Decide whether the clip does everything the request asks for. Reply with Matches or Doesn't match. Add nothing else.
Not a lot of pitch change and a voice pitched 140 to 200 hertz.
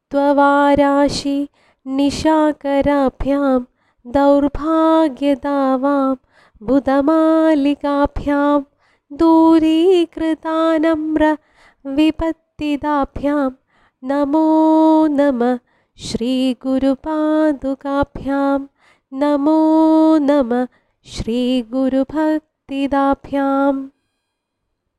Doesn't match